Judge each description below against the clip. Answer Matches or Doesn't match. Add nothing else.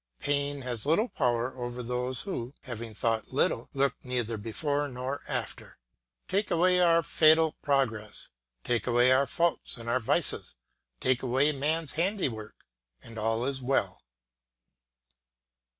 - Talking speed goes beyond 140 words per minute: Doesn't match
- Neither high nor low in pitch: Doesn't match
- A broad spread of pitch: Doesn't match